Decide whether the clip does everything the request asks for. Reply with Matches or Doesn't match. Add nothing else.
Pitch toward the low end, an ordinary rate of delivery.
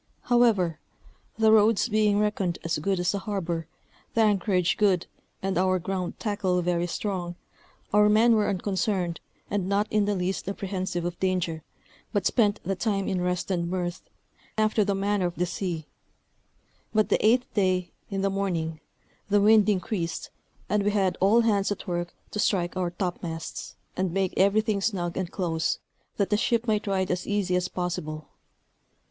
Doesn't match